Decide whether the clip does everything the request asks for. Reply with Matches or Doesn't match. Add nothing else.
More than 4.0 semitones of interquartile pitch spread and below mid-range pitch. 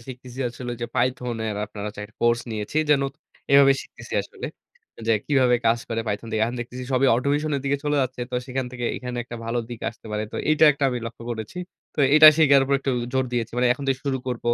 Doesn't match